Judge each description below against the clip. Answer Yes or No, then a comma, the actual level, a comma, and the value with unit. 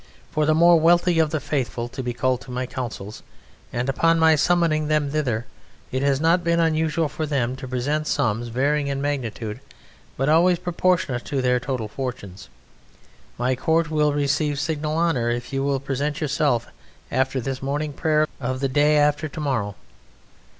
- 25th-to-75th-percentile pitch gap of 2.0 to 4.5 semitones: Yes, average, 3.4 semitones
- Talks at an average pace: Yes, average, 175 wpm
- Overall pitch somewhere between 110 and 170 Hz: Yes, medium, 140 Hz